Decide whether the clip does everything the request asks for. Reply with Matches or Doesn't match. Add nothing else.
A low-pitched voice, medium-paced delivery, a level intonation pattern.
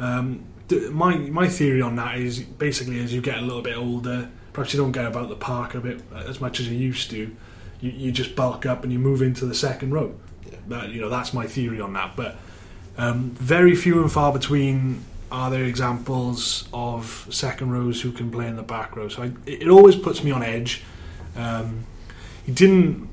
Doesn't match